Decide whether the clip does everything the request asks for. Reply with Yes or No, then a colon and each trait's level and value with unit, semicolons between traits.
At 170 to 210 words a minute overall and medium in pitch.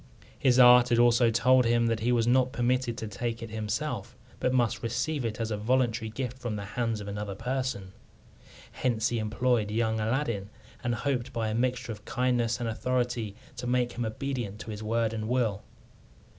No: average, 190 wpm; low, 120 Hz